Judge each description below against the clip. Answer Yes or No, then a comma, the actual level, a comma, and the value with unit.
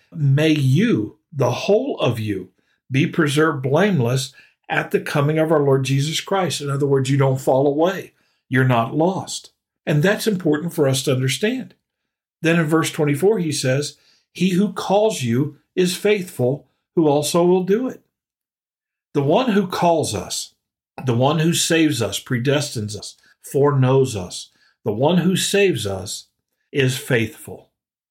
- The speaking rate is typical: Yes, average, 155 wpm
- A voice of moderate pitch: Yes, medium, 150 Hz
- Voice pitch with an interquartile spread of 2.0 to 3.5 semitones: No, average, 4.7 semitones